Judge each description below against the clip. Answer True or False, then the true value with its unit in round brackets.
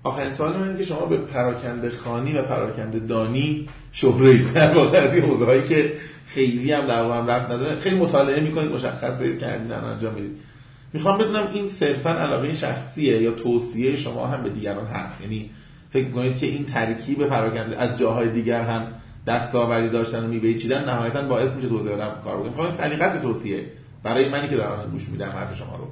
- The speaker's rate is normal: False (185 wpm)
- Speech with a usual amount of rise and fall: True (4.0 semitones)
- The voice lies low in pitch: True (130 Hz)